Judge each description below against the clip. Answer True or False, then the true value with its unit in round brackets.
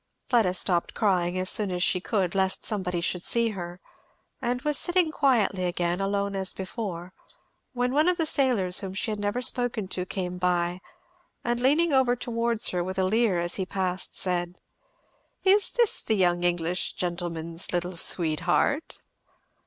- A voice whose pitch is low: False (190 Hz)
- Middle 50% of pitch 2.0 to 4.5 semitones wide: False (5.1 semitones)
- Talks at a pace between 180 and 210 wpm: False (165 wpm)